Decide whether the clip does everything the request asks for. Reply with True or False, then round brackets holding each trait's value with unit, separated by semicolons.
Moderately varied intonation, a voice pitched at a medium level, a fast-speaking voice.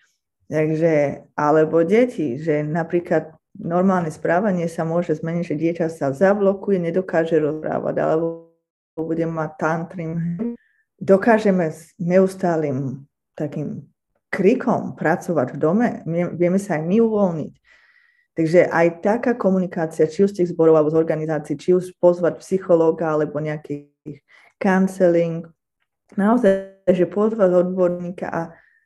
False (3.0 semitones; 170 Hz; 120 wpm)